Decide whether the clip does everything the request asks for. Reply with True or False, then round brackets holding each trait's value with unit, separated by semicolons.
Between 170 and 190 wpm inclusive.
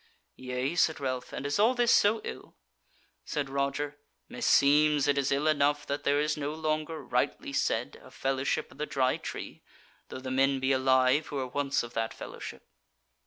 True (180 wpm)